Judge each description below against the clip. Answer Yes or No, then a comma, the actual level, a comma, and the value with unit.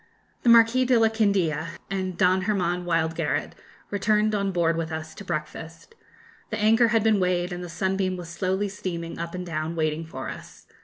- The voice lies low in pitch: No, medium, 180 Hz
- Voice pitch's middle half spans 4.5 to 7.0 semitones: No, average, 3.7 semitones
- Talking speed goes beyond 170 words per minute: Yes, average, 190 wpm